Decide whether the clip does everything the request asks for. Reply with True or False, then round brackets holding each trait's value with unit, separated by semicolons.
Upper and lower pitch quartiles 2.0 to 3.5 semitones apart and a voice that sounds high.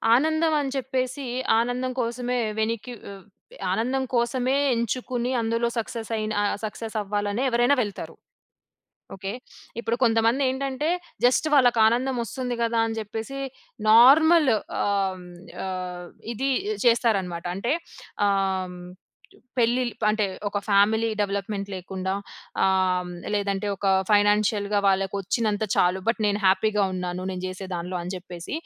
False (4.0 semitones; 220 Hz)